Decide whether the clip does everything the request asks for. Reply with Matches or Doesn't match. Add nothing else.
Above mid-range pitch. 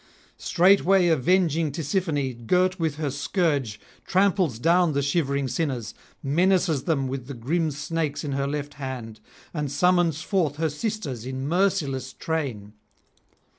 Doesn't match